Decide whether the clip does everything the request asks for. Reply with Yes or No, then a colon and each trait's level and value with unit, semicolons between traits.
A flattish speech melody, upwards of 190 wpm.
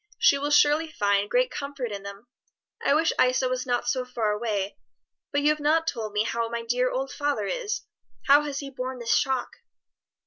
No: average, 4.1 semitones; average, 200 wpm